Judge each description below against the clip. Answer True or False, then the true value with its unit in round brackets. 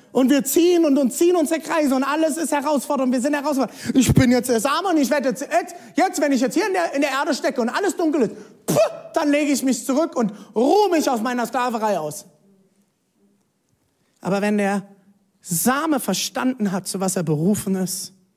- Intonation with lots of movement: True (7.0 semitones)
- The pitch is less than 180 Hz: False (260 Hz)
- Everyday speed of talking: False (210 wpm)